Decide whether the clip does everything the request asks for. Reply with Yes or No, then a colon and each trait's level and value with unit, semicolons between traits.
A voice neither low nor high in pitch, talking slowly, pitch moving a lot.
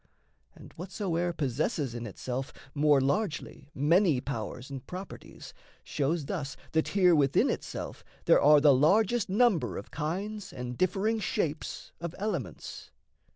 Yes: medium, 155 Hz; slow, 130 wpm; wide, 5.7 semitones